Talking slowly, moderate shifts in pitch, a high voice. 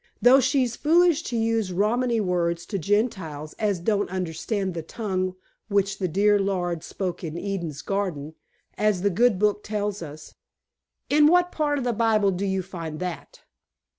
No: average, 165 wpm; average, 4.1 semitones; high, 200 Hz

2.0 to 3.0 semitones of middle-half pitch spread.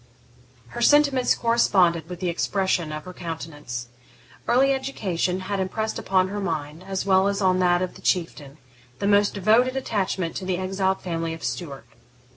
No: average, 3.4 semitones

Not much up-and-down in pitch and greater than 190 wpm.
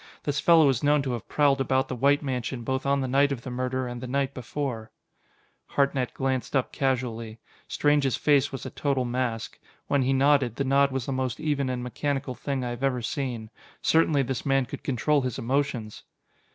Yes: narrow, 2.1 semitones; average, 200 wpm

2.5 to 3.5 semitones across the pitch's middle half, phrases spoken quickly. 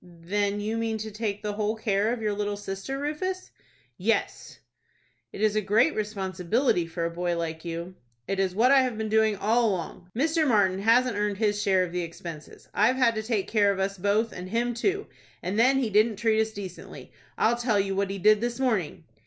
Yes: average, 3.0 semitones; fast, 210 wpm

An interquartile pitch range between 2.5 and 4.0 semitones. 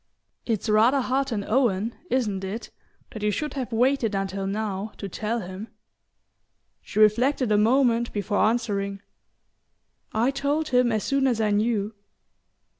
Yes: average, 3.6 semitones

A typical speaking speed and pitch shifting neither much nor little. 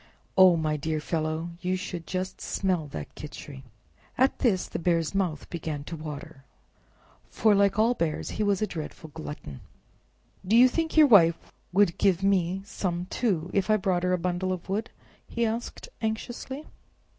Yes: average, 170 wpm; average, 4.1 semitones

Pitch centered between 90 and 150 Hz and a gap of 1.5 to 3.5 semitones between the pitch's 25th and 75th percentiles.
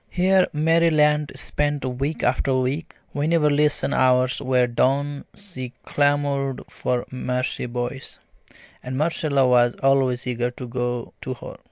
Yes: low, 135 Hz; average, 2.8 semitones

